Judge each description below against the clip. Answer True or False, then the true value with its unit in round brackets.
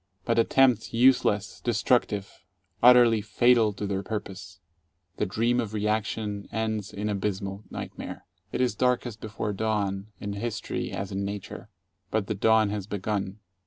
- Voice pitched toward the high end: False (105 Hz)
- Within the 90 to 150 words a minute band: True (140 wpm)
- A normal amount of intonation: False (1.9 semitones)